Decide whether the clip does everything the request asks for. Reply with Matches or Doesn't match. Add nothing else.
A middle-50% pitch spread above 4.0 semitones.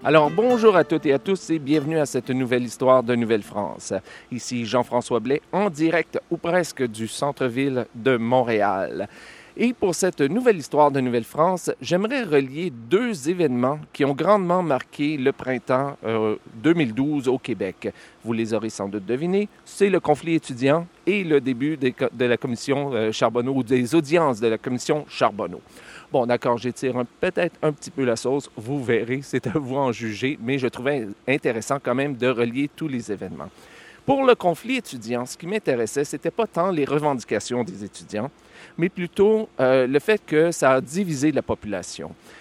Matches